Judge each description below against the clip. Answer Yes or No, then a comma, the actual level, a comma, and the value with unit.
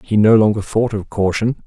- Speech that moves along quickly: Yes, fast, 215 wpm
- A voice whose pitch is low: Yes, low, 105 Hz